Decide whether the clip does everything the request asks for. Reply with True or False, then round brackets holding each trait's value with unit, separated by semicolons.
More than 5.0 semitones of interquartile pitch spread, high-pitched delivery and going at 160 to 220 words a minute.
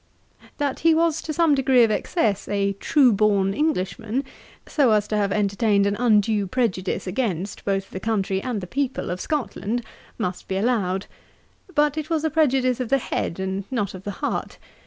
True (5.4 semitones; 215 Hz; 180 wpm)